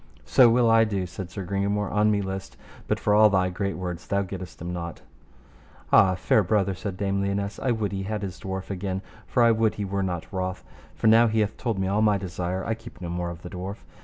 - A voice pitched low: Yes, low, 100 Hz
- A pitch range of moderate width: No, narrow, 2.3 semitones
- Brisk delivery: Yes, fast, 240 wpm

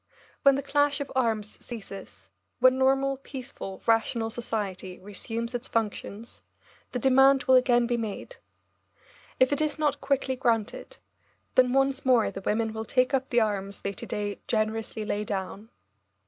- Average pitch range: Yes, average, 3.7 semitones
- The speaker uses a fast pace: No, average, 155 wpm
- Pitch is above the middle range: Yes, high, 240 Hz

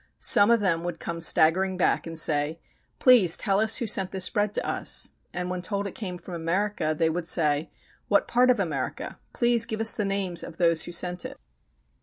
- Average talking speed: No, fast, 210 wpm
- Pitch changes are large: No, average, 3.7 semitones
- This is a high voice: No, medium, 180 Hz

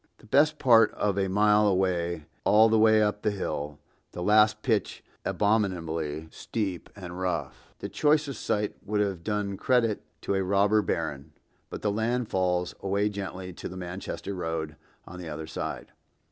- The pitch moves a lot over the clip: No, average, 3.3 semitones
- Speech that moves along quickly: No, average, 170 wpm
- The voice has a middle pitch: No, low, 100 Hz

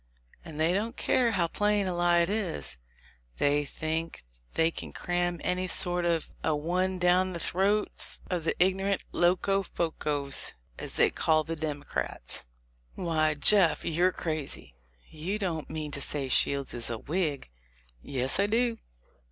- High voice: No, medium, 170 Hz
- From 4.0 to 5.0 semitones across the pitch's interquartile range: No, average, 3.5 semitones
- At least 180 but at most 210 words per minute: No, average, 150 wpm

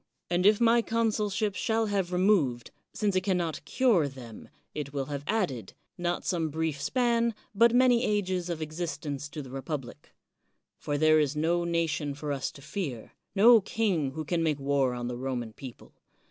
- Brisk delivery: No, average, 180 wpm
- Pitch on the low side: No, medium, 165 Hz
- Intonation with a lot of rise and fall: Yes, wide, 6.4 semitones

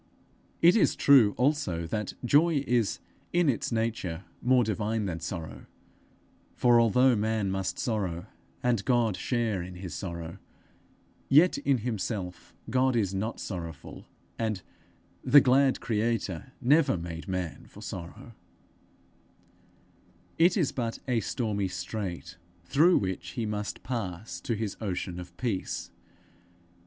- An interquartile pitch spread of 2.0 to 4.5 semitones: No, average, 5.3 semitones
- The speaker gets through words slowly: Yes, slow, 125 wpm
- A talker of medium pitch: No, low, 110 Hz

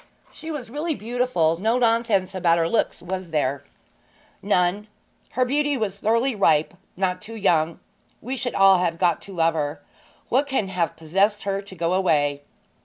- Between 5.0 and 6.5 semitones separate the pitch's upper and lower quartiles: Yes, wide, 5.5 semitones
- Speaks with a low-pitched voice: No, high, 195 Hz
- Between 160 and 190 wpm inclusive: Yes, average, 170 wpm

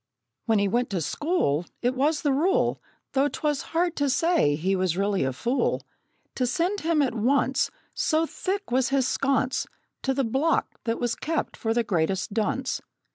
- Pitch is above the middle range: Yes, very high, 260 Hz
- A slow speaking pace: No, average, 180 wpm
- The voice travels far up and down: Yes, wide, 5.7 semitones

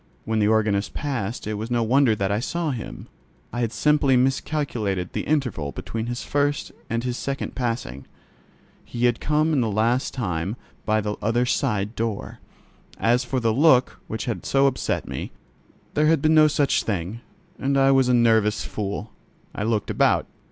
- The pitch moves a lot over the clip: No, average, 4.1 semitones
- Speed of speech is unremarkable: Yes, average, 180 wpm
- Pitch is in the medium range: No, low, 120 Hz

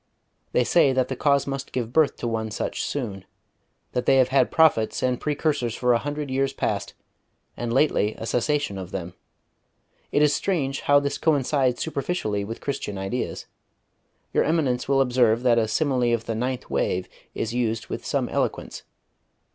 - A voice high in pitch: No, low, 125 Hz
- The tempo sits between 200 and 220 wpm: No, average, 170 wpm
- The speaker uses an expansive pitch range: No, average, 3.7 semitones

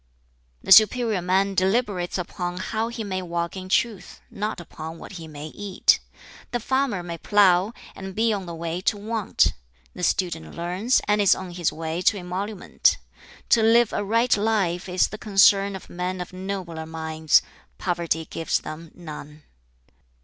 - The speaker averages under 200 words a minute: Yes, average, 165 wpm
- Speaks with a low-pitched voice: No, medium, 185 Hz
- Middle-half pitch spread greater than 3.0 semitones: Yes, average, 3.4 semitones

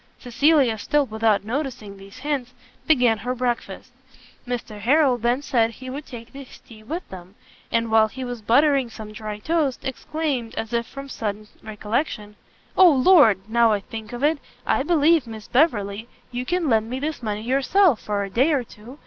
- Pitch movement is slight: No, average, 4.3 semitones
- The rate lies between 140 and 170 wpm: No, average, 180 wpm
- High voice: Yes, high, 240 Hz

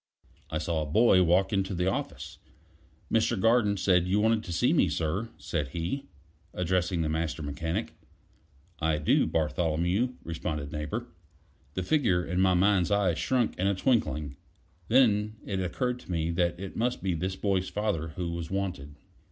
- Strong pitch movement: No, average, 4.0 semitones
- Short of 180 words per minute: Yes, average, 160 wpm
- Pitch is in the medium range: No, very low, 90 Hz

